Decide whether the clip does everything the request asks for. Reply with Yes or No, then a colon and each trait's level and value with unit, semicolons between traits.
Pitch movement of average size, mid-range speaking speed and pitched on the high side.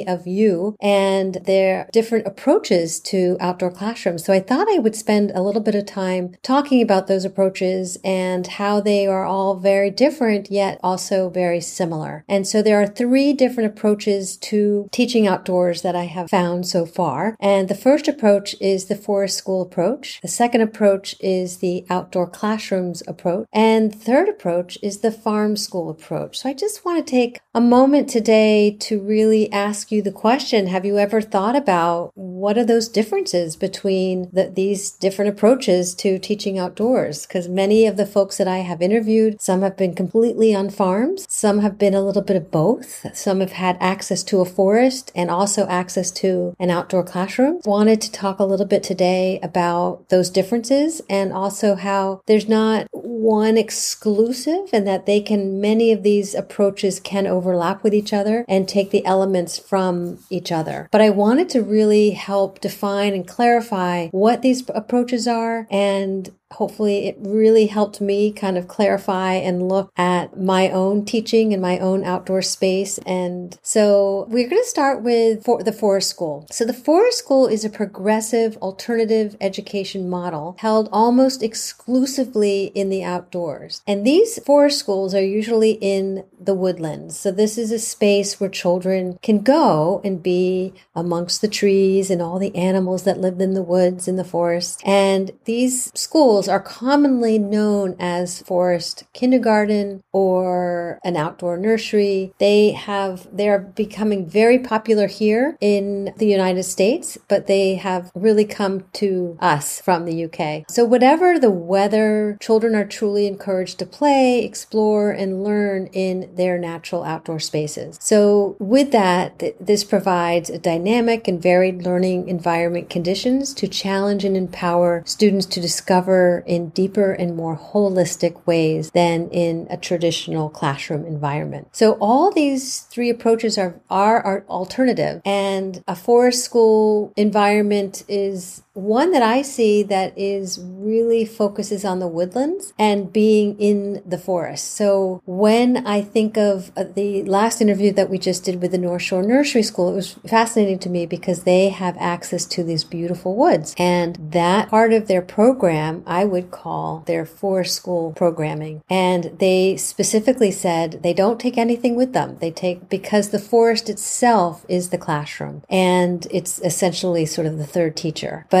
Yes: average, 3.0 semitones; average, 165 wpm; high, 195 Hz